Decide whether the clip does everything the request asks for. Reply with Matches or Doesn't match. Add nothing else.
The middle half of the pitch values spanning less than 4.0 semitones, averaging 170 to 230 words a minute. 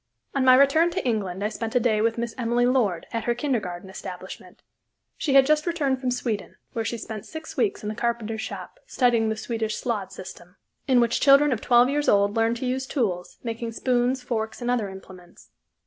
Matches